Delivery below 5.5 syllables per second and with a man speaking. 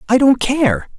Yes: 4.0 syllables/s; male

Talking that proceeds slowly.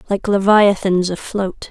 Yes: slow, 105 wpm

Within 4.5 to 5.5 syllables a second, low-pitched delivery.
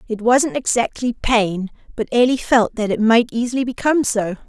No: 5.1 syllables/s; high, 235 Hz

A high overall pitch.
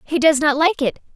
Yes: very high, 295 Hz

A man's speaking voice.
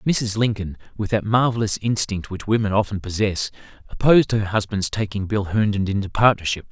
Yes: male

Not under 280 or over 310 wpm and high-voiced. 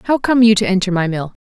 Yes: fast, 295 wpm; high, 200 Hz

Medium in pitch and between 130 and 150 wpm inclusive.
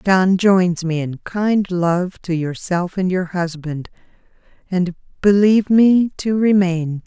Yes: medium, 180 Hz; slow, 135 wpm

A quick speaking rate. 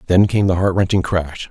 Yes: fast, 240 wpm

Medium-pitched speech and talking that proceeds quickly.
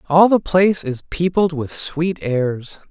No: medium, 160 Hz; average, 165 wpm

